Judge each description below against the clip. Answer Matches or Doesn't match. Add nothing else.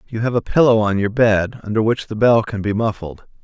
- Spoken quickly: Matches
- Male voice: Matches